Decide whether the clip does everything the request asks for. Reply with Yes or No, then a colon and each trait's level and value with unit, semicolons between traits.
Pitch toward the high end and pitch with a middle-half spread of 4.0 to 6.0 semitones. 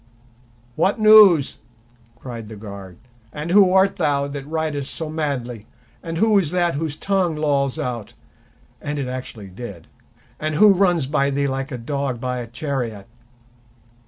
No: medium, 140 Hz; average, 5.0 semitones